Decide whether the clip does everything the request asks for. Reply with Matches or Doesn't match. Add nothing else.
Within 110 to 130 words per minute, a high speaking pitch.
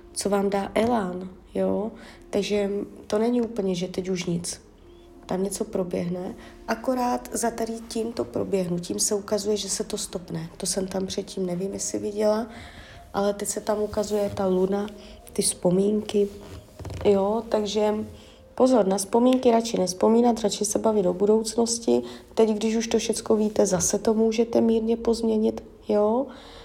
Doesn't match